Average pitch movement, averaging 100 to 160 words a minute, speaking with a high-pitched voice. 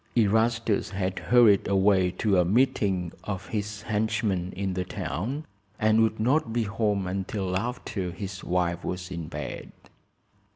No: average, 3.2 semitones; average, 140 wpm; low, 100 Hz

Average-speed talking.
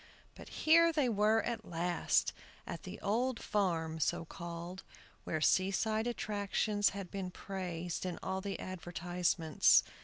No: slow, 130 wpm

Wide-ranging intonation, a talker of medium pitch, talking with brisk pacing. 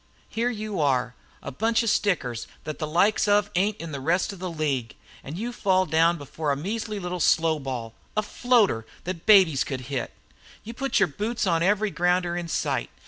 No: wide, 5.7 semitones; medium, 175 Hz; average, 195 wpm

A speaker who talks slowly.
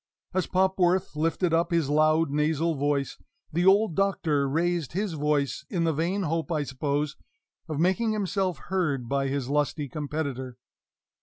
No: average, 150 wpm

